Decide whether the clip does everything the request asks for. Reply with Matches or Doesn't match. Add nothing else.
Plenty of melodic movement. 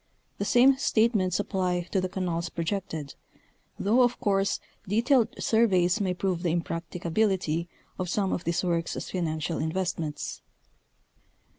Doesn't match